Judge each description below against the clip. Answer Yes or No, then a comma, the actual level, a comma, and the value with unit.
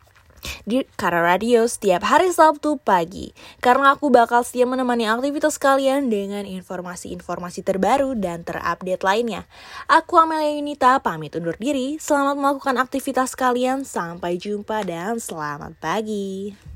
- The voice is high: Yes, high, 235 Hz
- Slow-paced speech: No, average, 125 wpm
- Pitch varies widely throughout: Yes, wide, 6.7 semitones